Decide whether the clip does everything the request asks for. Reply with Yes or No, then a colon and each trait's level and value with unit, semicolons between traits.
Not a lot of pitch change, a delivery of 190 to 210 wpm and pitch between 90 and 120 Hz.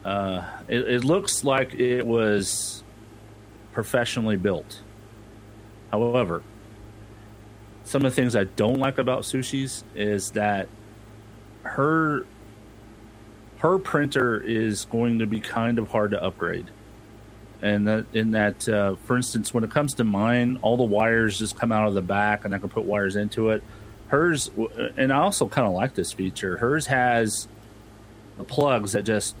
No: narrow, 2.2 semitones; average, 155 wpm; low, 110 Hz